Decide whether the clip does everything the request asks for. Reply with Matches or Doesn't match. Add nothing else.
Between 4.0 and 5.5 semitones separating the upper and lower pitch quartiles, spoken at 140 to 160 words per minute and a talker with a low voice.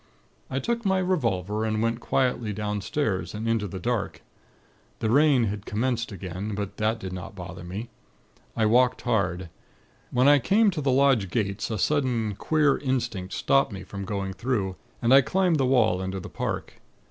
Doesn't match